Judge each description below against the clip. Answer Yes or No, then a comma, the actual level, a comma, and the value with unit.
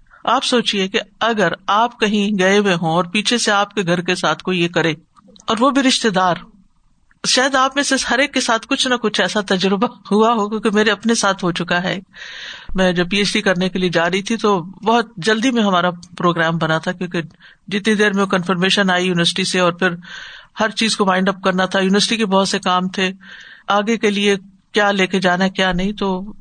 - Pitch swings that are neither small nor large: Yes, average, 3.1 semitones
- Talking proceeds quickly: Yes, fast, 225 wpm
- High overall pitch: Yes, high, 200 Hz